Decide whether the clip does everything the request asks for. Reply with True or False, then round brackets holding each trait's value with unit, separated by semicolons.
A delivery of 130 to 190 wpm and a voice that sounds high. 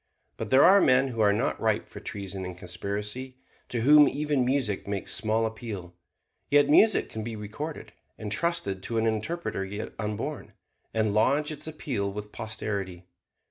False (160 wpm; 110 Hz)